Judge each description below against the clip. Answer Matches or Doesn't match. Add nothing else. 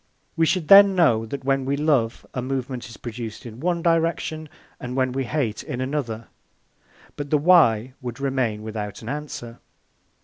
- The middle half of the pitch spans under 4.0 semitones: Doesn't match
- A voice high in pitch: Doesn't match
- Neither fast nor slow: Matches